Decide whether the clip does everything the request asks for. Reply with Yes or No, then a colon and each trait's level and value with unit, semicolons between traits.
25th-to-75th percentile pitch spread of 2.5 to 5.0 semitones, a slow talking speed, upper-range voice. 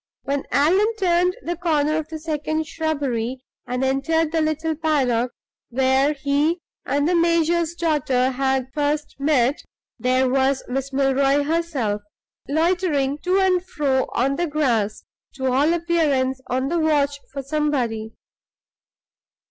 Yes: average, 3.4 semitones; slow, 130 wpm; very high, 290 Hz